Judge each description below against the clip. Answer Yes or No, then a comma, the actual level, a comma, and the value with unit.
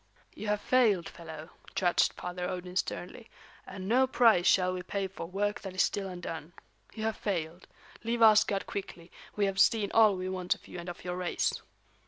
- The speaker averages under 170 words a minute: No, average, 190 wpm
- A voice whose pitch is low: No, medium, 185 Hz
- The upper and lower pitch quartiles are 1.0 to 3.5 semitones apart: Yes, average, 2.8 semitones